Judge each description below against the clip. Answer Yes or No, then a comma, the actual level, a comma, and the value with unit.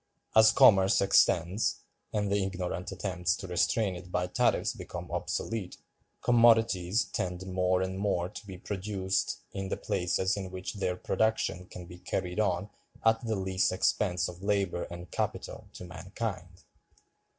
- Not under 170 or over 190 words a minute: No, average, 150 wpm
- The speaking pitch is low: Yes, very low, 95 Hz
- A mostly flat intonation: Yes, narrow, 2.2 semitones